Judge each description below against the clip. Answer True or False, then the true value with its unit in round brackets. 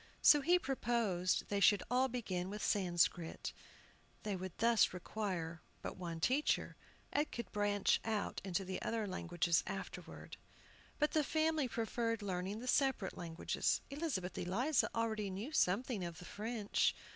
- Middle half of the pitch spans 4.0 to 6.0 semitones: True (5.1 semitones)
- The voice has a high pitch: True (205 Hz)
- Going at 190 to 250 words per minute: False (145 wpm)